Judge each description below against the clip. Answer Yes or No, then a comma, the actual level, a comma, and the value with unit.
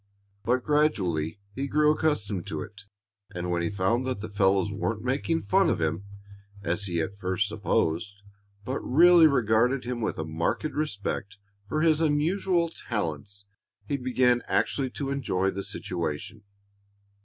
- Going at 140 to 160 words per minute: Yes, average, 150 wpm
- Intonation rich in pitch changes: Yes, wide, 6.5 semitones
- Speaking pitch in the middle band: No, low, 105 Hz